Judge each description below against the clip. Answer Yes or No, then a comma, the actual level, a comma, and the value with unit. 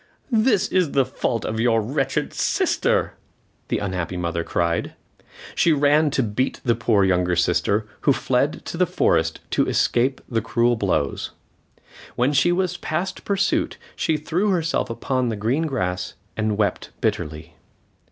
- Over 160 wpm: No, average, 150 wpm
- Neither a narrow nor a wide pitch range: No, wide, 7.3 semitones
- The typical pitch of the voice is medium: No, low, 120 Hz